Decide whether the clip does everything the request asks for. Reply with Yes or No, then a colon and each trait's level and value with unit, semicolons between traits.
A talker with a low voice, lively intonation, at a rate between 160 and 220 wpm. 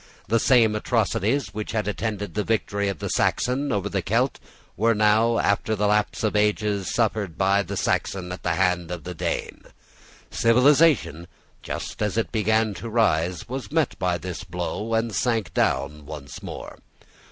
No: low, 105 Hz; average, 3.7 semitones; average, 165 wpm